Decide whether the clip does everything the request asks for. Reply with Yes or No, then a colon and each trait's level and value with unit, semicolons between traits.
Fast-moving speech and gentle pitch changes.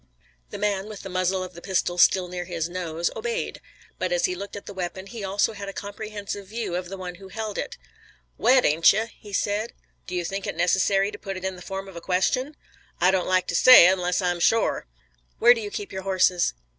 Yes: fast, 230 wpm; narrow, 2.3 semitones